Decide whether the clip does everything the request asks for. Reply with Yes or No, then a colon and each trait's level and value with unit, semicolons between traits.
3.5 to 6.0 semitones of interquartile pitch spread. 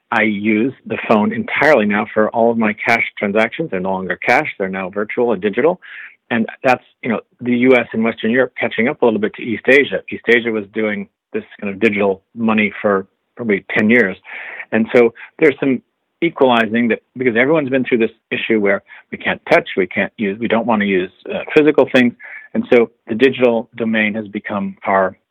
No: narrow, 2.5 semitones